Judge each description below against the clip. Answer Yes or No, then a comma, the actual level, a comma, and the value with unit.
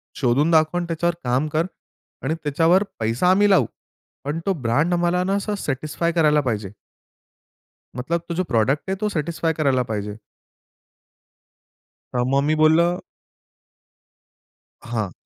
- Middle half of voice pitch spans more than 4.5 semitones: Yes, average, 4.9 semitones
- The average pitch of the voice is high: No, medium, 155 Hz